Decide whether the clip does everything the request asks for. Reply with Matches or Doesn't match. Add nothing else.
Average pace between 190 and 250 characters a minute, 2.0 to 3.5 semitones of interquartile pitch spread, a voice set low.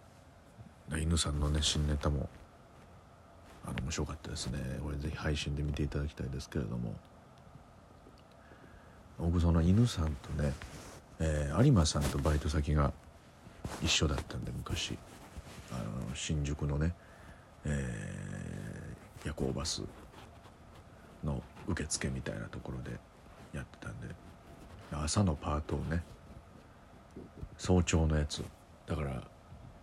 Matches